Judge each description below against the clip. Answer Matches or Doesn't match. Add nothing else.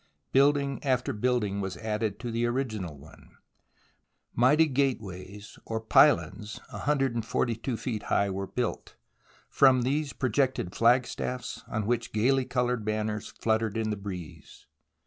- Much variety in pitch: Doesn't match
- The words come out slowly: Matches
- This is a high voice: Doesn't match